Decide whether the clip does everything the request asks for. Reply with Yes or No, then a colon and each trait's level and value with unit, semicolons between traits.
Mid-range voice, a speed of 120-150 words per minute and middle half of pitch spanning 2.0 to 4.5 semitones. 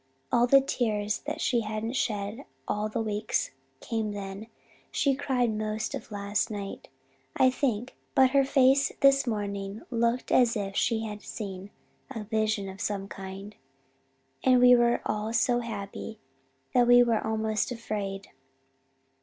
No: high, 220 Hz; average, 145 wpm; average, 3.0 semitones